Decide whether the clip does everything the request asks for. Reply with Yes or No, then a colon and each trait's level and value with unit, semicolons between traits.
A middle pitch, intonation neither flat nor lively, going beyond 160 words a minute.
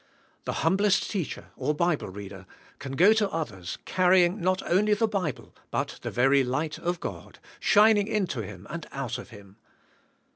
No: medium, 170 Hz; wide, 7.9 semitones; average, 170 wpm